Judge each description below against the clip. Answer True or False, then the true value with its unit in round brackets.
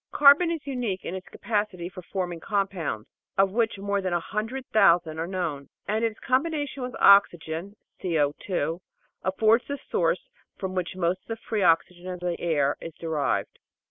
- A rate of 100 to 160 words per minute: False (175 wpm)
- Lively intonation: False (4.3 semitones)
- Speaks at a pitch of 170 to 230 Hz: True (190 Hz)